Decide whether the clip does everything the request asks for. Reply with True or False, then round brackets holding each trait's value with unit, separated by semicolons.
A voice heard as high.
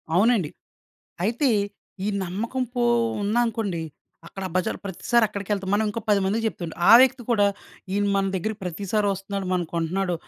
True (200 Hz)